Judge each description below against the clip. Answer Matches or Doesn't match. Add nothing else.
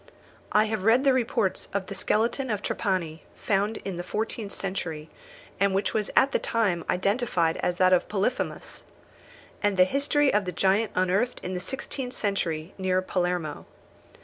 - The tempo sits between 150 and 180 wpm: Matches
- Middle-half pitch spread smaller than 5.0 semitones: Matches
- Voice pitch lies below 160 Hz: Doesn't match